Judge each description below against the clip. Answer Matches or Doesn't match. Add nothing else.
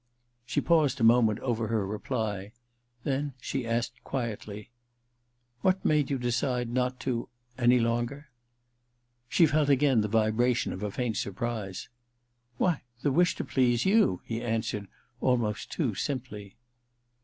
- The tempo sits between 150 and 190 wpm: Matches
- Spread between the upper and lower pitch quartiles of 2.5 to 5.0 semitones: Matches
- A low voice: Matches